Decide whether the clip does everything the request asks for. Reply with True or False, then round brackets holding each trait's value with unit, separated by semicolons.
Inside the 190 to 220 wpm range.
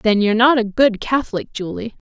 True (200 wpm)